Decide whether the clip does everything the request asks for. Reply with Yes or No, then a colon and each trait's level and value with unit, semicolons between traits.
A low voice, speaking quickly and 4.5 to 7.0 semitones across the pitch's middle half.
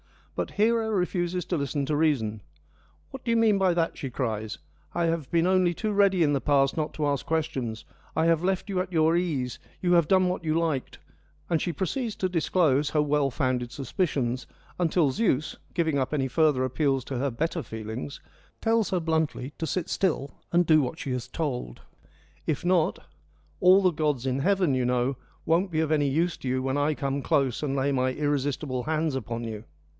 No: medium, 150 Hz; fast, 210 wpm; average, 4.8 semitones